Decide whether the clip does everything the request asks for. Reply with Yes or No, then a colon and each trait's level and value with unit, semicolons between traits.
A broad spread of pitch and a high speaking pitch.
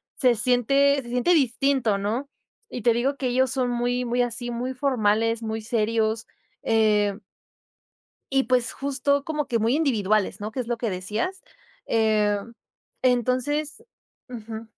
No: average, 3.0 semitones; high, 240 Hz